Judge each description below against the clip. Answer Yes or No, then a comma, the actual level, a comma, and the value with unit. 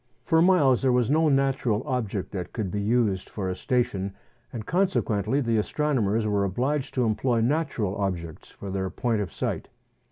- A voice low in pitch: Yes, low, 115 Hz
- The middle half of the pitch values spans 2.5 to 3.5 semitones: No, average, 5.2 semitones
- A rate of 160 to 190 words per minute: Yes, average, 170 wpm